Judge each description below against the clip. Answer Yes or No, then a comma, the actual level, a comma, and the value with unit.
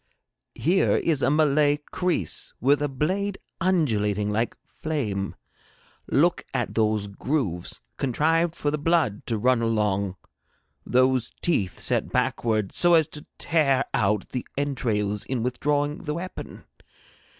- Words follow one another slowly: Yes, slow, 130 wpm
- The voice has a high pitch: No, low, 130 Hz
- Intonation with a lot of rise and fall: Yes, wide, 6.4 semitones